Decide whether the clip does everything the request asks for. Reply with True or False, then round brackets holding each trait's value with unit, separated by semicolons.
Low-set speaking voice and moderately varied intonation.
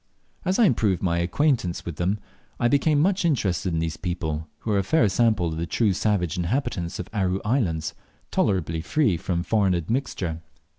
False (95 Hz; 5.7 semitones)